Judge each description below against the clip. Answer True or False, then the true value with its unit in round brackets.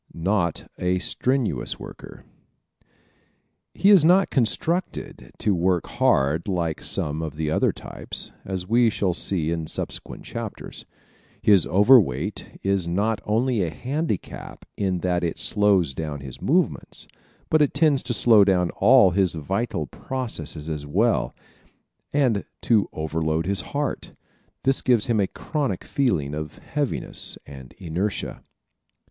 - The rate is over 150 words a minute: False (135 wpm)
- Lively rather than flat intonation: True (6.9 semitones)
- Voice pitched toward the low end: True (95 Hz)